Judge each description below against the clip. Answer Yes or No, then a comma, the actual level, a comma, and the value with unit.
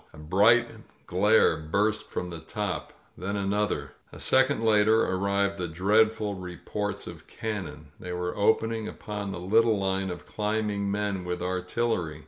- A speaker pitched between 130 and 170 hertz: No, low, 100 Hz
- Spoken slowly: No, average, 155 wpm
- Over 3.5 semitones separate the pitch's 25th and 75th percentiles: No, average, 3.0 semitones